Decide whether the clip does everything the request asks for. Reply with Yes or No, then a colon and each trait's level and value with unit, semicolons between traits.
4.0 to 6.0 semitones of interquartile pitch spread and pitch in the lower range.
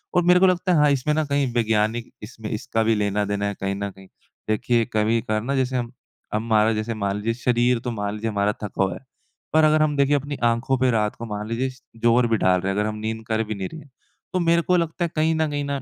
Yes: average, 4.9 semitones; low, 115 Hz